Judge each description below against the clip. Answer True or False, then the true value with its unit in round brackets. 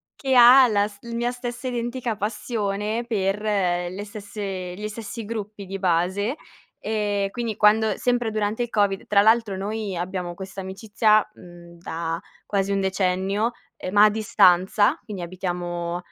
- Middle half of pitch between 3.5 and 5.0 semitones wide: False (2.8 semitones)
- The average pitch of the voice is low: False (205 Hz)